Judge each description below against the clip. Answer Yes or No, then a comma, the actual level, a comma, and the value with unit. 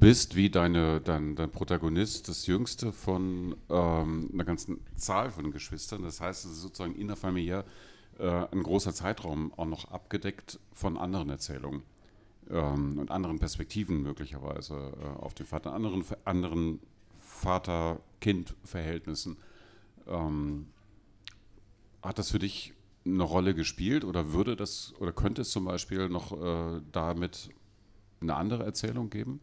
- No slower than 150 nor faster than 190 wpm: No, average, 135 wpm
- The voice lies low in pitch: Yes, very low, 90 Hz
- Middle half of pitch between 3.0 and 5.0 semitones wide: Yes, average, 3.9 semitones